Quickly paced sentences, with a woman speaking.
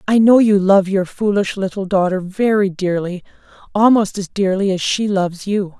No: average, 175 wpm; female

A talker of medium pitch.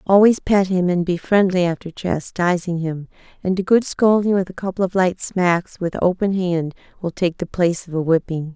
Yes: medium, 180 Hz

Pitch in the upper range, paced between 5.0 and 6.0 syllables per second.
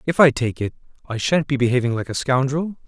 No: low, 135 Hz; 5.9 syllables/s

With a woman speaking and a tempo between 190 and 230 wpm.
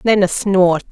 Yes: female; average, 200 wpm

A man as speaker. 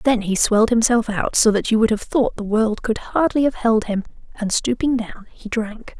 No: female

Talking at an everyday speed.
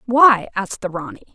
Yes: average, 180 wpm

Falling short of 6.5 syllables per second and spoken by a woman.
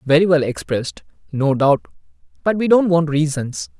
No: 5.0 syllables/s; male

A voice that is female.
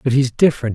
No: male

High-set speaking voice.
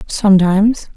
Yes: high, 200 Hz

